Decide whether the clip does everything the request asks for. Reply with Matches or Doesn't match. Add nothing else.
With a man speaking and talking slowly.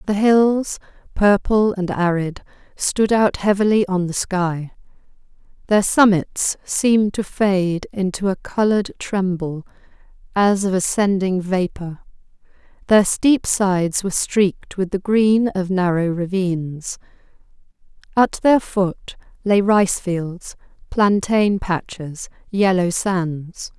Doesn't match